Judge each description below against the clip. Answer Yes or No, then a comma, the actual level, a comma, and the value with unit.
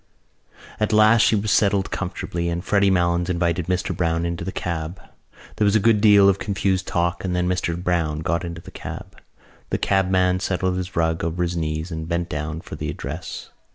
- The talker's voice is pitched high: No, very low, 90 Hz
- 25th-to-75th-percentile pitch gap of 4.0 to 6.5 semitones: No, narrow, 2.4 semitones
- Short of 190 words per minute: No, average, 195 wpm